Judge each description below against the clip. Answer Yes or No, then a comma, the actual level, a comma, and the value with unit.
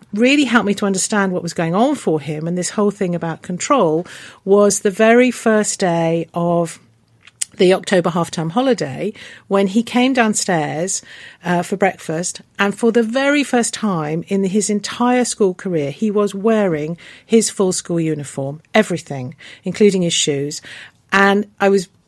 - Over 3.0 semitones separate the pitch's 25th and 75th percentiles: Yes, average, 4.3 semitones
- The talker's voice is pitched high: Yes, high, 195 Hz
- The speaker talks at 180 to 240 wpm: No, average, 165 wpm